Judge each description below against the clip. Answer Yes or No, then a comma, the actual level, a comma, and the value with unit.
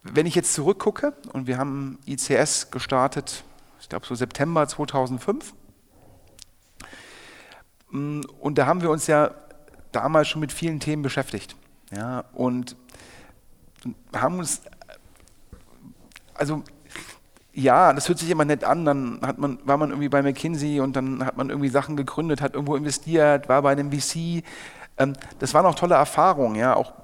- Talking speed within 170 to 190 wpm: No, average, 150 wpm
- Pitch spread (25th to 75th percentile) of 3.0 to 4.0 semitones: No, narrow, 2.4 semitones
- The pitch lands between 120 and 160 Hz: Yes, medium, 140 Hz